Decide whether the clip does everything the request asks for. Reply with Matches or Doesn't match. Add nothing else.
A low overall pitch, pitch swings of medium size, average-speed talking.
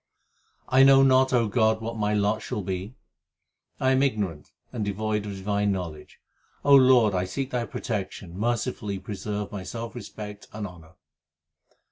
Matches